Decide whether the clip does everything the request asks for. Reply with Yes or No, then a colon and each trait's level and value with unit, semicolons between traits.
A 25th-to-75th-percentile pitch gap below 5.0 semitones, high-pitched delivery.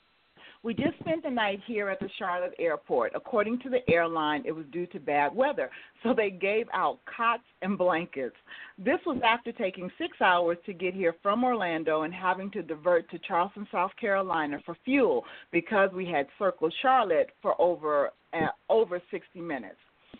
No: average, 5.3 semitones; high, 195 Hz